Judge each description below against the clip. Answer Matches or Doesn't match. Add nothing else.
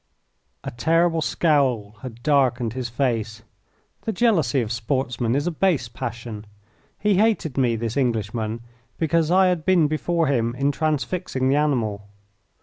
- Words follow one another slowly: Doesn't match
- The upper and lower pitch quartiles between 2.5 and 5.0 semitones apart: Doesn't match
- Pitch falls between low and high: Doesn't match